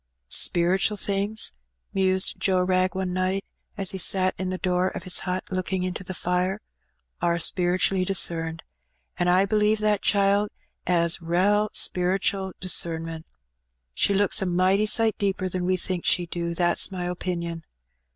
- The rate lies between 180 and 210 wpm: No, average, 155 wpm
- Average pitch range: No, narrow, 1.6 semitones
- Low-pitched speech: No, medium, 185 Hz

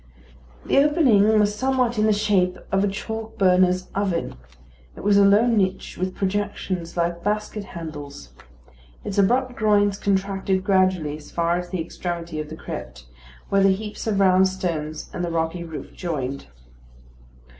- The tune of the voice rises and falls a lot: No, average, 3.3 semitones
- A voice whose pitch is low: No, high, 190 Hz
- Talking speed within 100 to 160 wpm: Yes, average, 155 wpm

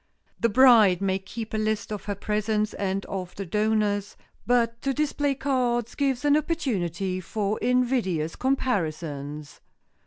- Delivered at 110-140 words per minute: Yes, slow, 135 wpm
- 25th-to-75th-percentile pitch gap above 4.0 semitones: Yes, average, 4.7 semitones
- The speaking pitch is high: Yes, high, 215 Hz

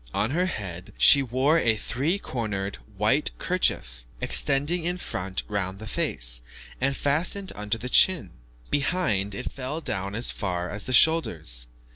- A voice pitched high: No, low, 115 Hz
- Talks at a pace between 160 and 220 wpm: No, average, 150 wpm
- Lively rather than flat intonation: Yes, wide, 7.7 semitones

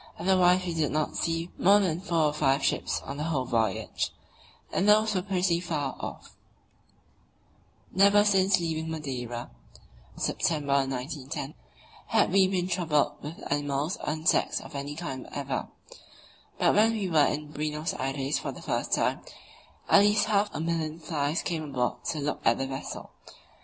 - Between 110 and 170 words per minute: Yes, average, 160 wpm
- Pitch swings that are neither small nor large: Yes, average, 4.4 semitones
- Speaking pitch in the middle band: Yes, medium, 160 Hz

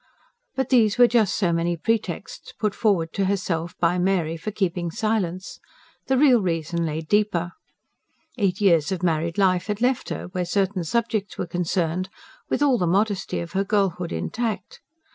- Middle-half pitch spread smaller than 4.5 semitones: Yes, average, 3.8 semitones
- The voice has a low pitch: No, medium, 185 Hz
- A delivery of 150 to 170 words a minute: Yes, average, 165 wpm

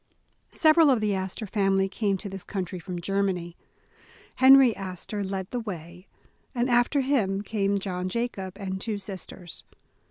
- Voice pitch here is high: Yes, high, 195 Hz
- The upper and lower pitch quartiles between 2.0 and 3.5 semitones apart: Yes, average, 3.1 semitones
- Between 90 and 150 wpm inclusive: No, average, 160 wpm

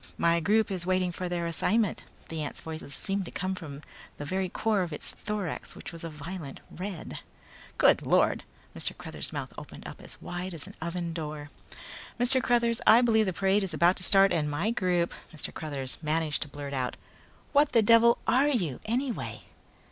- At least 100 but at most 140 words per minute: No, average, 195 wpm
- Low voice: No, medium, 180 Hz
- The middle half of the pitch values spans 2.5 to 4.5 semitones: No, average, 5.0 semitones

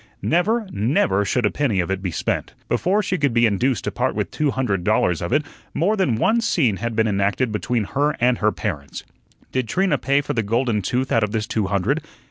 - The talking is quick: Yes, fast, 225 wpm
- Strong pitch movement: Yes, wide, 5.9 semitones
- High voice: No, low, 115 Hz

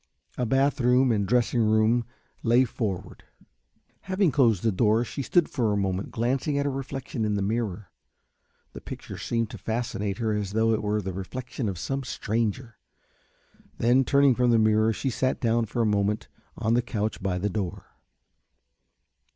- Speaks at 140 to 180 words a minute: Yes, average, 175 wpm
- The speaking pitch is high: No, low, 115 Hz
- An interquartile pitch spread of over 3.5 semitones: No, average, 3.2 semitones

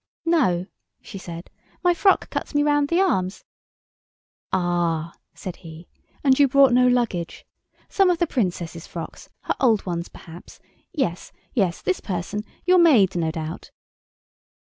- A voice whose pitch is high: Yes, high, 195 Hz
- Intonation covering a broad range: Yes, wide, 9.0 semitones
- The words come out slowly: Yes, slow, 120 wpm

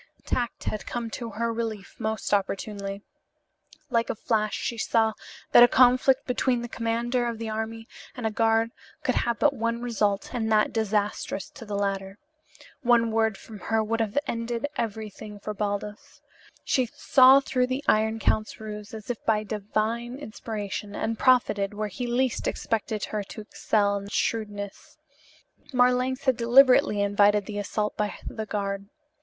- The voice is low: No, high, 220 Hz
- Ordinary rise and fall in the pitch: No, narrow, 2.3 semitones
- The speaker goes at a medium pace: Yes, average, 160 wpm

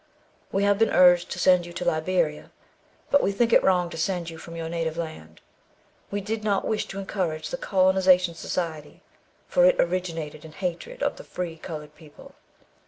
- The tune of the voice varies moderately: Yes, average, 3.2 semitones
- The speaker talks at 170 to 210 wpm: Yes, average, 185 wpm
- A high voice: No, medium, 180 Hz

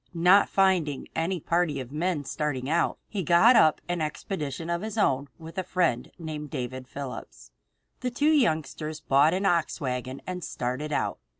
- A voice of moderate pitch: Yes, medium, 155 Hz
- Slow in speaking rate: No, average, 185 wpm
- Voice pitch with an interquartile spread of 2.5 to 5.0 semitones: Yes, average, 4.6 semitones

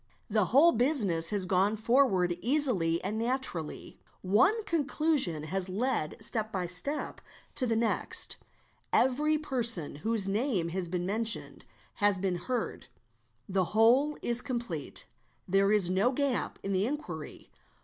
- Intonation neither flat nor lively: No, wide, 5.8 semitones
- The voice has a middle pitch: No, high, 215 Hz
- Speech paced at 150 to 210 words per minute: No, slow, 135 wpm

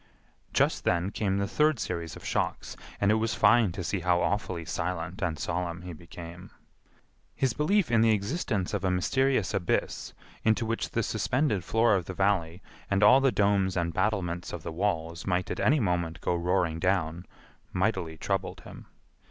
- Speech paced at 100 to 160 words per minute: No, average, 175 wpm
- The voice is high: No, very low, 95 Hz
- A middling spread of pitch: Yes, average, 3.8 semitones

